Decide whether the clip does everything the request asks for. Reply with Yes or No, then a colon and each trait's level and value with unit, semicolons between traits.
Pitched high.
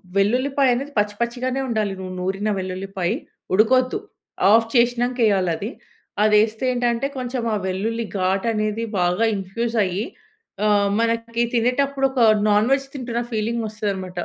Yes: high, 225 Hz